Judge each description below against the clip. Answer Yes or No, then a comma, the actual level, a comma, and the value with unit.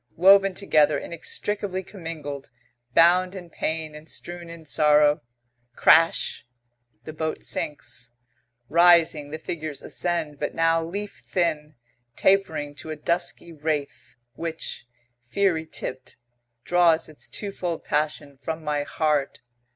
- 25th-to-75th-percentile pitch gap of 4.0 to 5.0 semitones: No, narrow, 2.5 semitones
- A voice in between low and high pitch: Yes, medium, 160 Hz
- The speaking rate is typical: No, slow, 115 wpm